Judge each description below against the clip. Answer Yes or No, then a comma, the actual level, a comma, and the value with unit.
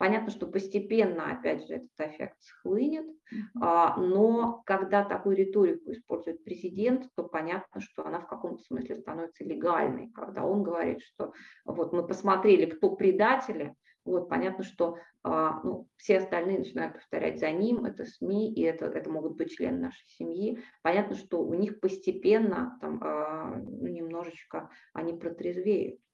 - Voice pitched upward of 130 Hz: Yes, high, 190 Hz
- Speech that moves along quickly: No, average, 145 wpm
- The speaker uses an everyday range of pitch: Yes, average, 4.5 semitones